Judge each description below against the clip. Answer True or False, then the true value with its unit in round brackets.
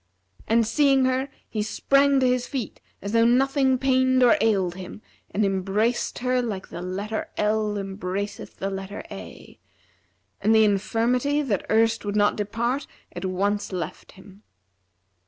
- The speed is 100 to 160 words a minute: True (150 wpm)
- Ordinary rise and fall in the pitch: True (4.1 semitones)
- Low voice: False (220 Hz)